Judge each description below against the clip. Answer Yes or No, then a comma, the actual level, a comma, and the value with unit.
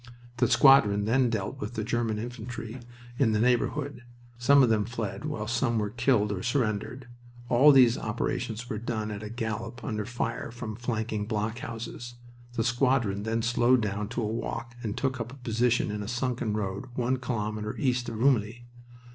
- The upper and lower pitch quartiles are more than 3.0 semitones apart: No, narrow, 2.5 semitones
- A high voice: No, low, 115 Hz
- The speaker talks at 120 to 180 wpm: Yes, average, 175 wpm